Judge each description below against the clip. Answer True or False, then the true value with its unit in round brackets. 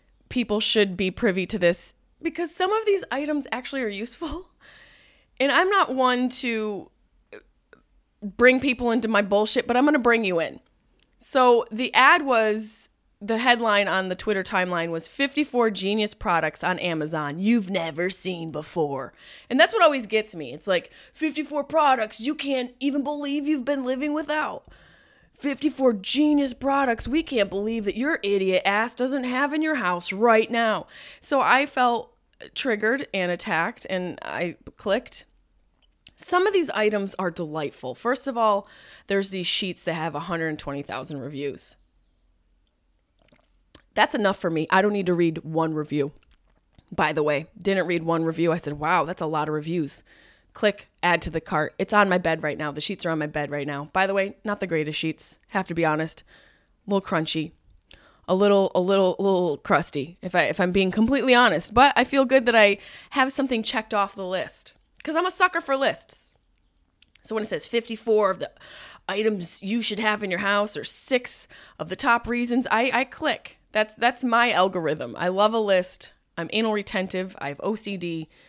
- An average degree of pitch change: False (6.3 semitones)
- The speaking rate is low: False (185 wpm)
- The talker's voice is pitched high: True (205 Hz)